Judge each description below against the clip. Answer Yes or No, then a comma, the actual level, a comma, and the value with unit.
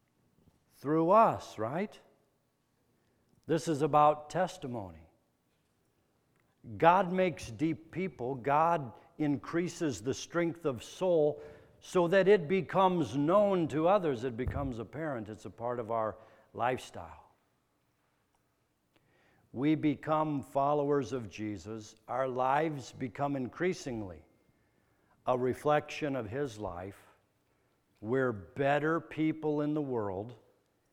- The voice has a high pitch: No, medium, 140 Hz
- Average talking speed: No, slow, 105 wpm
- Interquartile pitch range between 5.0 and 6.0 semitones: Yes, average, 5.3 semitones